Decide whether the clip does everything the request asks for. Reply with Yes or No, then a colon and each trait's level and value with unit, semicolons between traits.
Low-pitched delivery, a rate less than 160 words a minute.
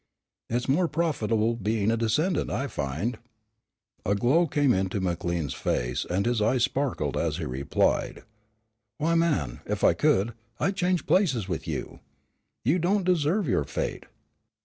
Yes: low, 115 Hz; average, 150 wpm